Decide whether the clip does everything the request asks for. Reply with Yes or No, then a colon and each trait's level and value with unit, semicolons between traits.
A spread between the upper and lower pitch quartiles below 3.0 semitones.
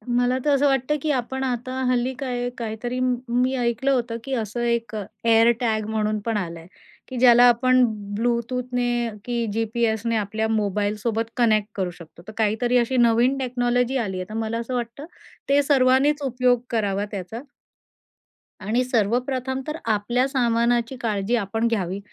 Yes: narrow, 2.5 semitones